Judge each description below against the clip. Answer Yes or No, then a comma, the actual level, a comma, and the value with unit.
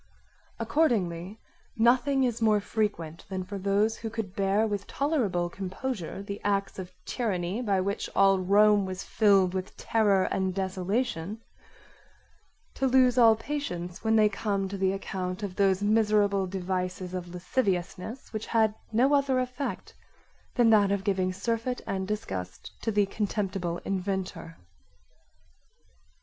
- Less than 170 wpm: Yes, slow, 135 wpm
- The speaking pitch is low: No, high, 200 Hz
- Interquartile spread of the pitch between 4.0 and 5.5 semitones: No, average, 3.1 semitones